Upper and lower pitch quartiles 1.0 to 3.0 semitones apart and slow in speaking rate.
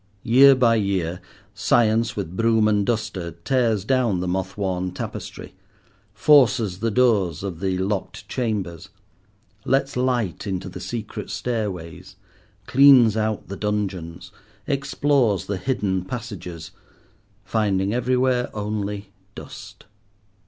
No: average, 4.2 semitones; slow, 110 wpm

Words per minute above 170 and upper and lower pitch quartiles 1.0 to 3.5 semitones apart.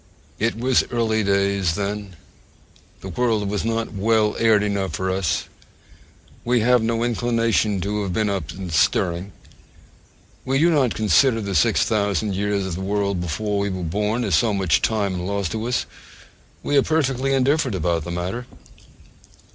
No: average, 165 wpm; average, 3.2 semitones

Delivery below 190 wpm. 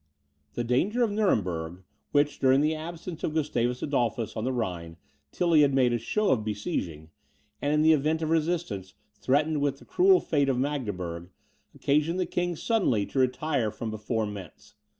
Yes: average, 170 wpm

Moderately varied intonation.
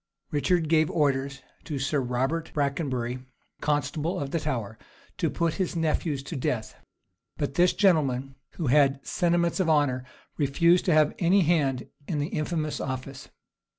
Yes: average, 3.6 semitones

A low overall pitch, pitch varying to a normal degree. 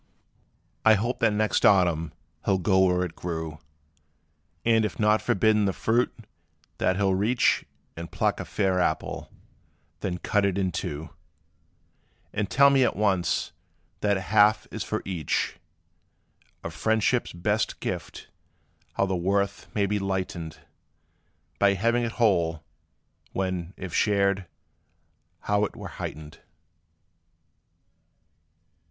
Yes: low, 100 Hz; average, 3.0 semitones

